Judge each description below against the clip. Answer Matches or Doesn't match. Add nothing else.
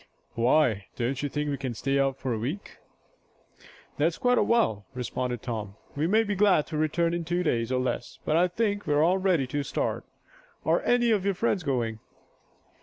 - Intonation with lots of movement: Matches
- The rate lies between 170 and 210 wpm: Matches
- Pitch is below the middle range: Doesn't match